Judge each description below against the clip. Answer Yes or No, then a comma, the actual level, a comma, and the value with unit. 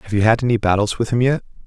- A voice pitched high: No, low, 115 Hz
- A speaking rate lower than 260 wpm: No, fast, 290 wpm